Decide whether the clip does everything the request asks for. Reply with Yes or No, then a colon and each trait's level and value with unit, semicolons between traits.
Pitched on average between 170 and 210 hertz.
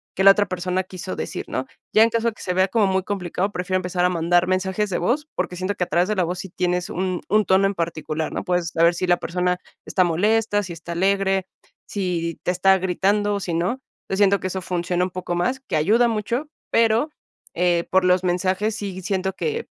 Yes: medium, 185 Hz